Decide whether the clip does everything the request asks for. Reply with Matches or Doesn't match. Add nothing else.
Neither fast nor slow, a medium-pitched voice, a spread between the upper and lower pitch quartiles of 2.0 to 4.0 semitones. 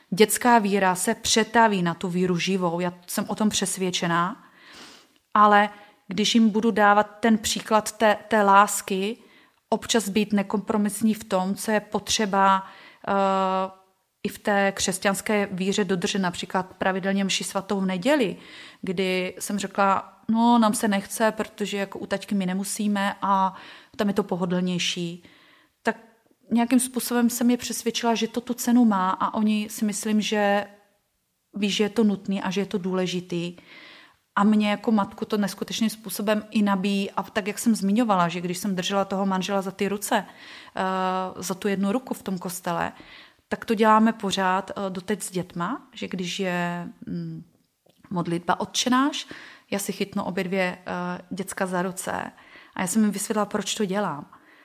Doesn't match